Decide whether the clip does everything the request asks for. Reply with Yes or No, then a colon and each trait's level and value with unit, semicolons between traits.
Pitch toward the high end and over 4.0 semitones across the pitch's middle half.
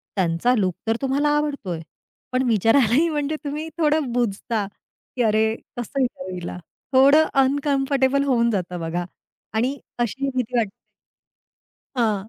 Yes: high, 245 Hz; average, 4.8 semitones